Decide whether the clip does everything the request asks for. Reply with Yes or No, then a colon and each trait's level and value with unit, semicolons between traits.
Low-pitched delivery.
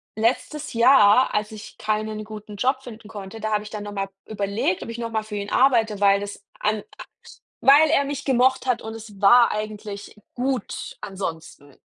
No: high, 215 Hz